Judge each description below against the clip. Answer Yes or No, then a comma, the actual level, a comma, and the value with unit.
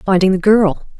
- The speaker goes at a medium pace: Yes, average, 180 wpm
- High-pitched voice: Yes, high, 195 Hz